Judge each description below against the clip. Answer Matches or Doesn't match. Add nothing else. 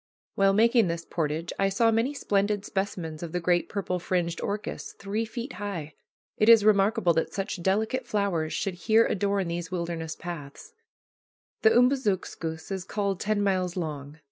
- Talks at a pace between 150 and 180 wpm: Matches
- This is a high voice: Matches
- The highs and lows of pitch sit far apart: Doesn't match